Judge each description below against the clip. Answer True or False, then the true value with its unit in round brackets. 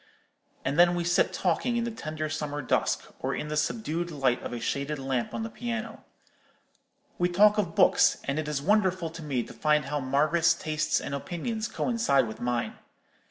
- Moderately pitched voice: True (155 Hz)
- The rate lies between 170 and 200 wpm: True (190 wpm)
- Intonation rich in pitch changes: False (4.7 semitones)